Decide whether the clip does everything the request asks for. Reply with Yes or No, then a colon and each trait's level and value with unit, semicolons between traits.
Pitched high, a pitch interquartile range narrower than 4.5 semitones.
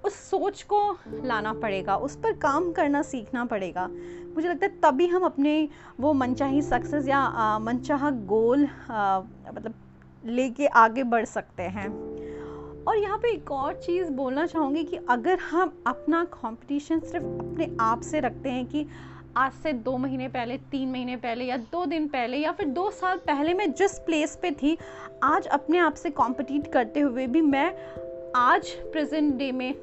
No: very high, 285 Hz; average, 5.0 semitones